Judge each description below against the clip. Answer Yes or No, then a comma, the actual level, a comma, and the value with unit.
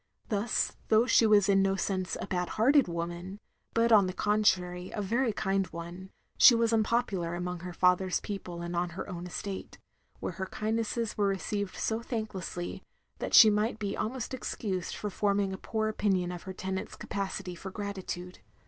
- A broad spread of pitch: No, average, 3.1 semitones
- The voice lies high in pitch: Yes, high, 195 Hz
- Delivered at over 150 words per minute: Yes, average, 175 wpm